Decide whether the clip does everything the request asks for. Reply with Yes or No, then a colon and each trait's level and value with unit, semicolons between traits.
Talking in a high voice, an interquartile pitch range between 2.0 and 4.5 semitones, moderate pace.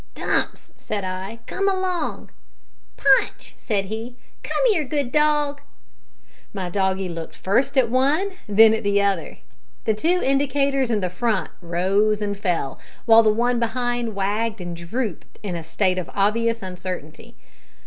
No: high, 220 Hz; average, 5.2 semitones; average, 145 wpm